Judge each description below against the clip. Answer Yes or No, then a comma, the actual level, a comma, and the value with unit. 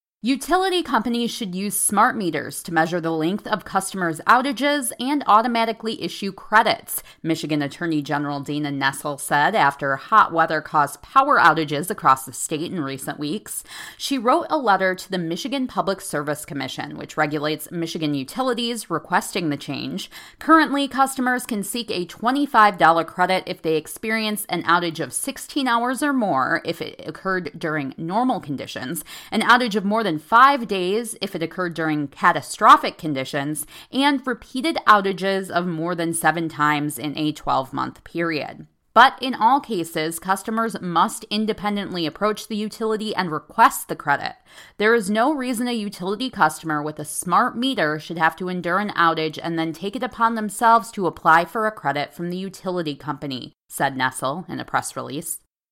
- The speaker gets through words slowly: No, average, 165 wpm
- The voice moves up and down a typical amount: No, wide, 6.4 semitones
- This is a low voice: No, medium, 180 Hz